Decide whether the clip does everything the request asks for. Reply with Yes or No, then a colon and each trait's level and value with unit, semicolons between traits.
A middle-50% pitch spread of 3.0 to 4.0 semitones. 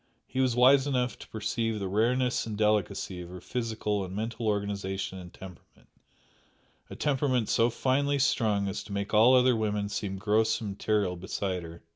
Yes: average, 3.7 semitones